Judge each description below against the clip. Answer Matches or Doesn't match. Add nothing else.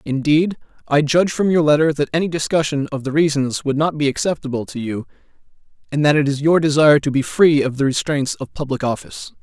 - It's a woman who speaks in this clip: Doesn't match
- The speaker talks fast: Matches